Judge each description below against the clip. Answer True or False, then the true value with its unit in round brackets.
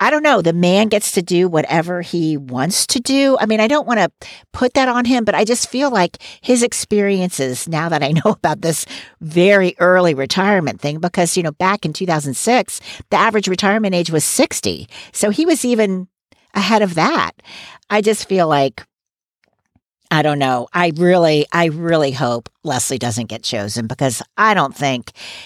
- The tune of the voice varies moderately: False (6.0 semitones)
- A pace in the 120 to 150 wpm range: False (185 wpm)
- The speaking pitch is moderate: True (180 Hz)